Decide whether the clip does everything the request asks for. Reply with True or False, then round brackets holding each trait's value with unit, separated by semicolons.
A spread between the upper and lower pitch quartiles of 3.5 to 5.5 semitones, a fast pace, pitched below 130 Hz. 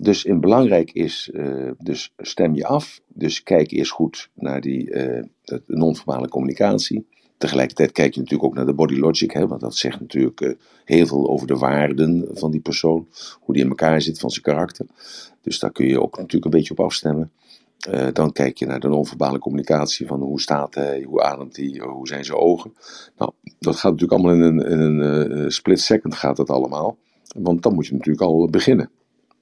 False (2.9 semitones; 205 wpm; 75 Hz)